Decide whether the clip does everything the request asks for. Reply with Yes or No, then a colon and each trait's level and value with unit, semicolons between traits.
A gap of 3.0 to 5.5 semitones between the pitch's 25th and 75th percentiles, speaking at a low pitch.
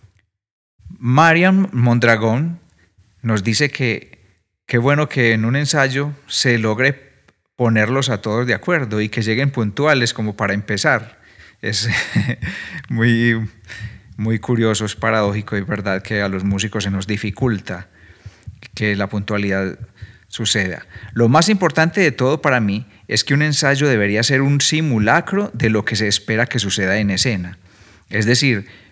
Yes: average, 4.0 semitones; low, 110 Hz